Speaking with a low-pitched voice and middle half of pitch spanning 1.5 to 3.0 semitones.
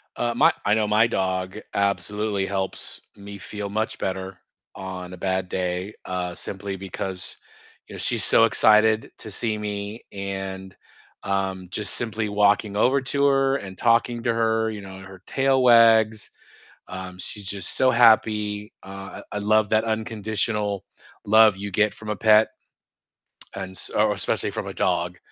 Yes: low, 105 Hz; narrow, 2.5 semitones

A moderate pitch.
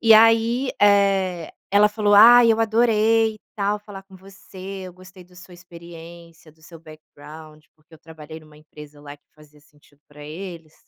Yes: medium, 180 Hz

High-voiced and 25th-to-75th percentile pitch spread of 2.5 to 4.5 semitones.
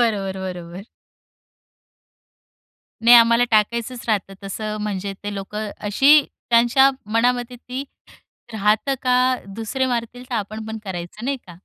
Yes: high, 220 Hz; average, 3.6 semitones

